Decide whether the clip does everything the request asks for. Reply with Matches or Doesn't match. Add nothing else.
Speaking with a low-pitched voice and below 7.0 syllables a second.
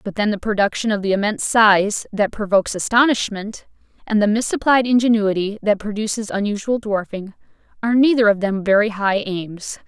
Doesn't match